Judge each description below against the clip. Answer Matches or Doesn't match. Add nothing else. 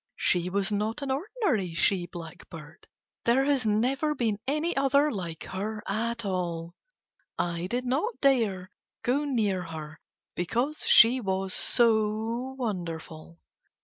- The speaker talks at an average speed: Doesn't match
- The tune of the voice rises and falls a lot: Matches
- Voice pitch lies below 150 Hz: Doesn't match